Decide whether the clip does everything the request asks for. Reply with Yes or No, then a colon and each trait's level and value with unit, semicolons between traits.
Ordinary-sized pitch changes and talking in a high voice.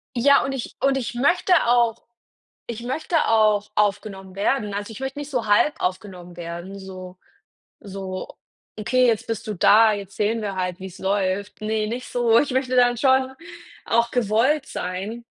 Yes: average, 4.1 semitones; high, 220 Hz